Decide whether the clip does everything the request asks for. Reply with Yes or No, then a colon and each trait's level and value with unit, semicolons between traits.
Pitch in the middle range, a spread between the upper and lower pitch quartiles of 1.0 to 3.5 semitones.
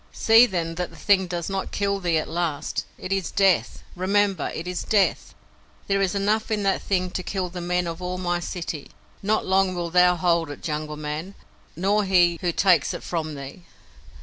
Yes: medium, 180 Hz; narrow, 2.5 semitones